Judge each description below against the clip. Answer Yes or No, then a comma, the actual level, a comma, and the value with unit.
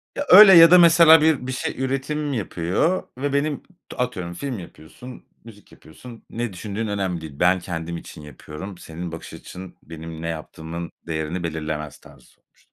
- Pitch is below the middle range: Yes, very low, 95 Hz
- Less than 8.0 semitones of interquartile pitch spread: No, wide, 8.6 semitones